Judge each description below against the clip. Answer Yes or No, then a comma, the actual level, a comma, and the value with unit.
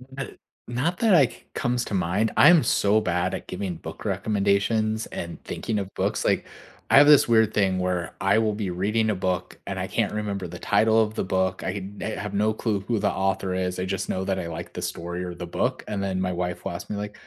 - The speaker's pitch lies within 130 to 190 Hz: No, low, 100 Hz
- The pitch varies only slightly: No, average, 3.1 semitones